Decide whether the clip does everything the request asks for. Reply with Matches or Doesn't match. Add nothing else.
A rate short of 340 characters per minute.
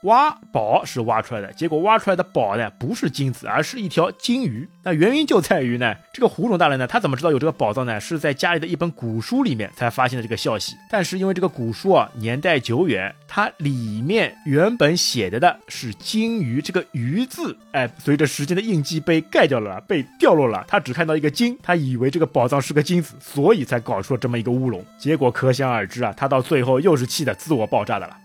Doesn't match